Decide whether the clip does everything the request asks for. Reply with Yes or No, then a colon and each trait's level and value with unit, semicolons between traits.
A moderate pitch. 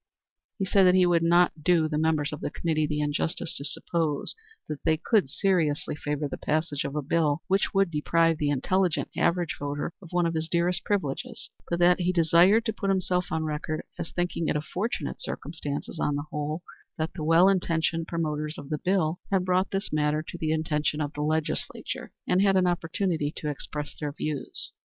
Yes: medium, 160 Hz